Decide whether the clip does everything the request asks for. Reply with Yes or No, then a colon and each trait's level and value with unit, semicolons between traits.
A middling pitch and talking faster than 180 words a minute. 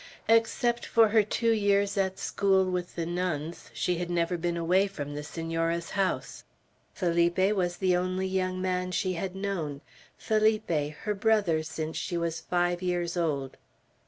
No: medium, 180 Hz; average, 160 wpm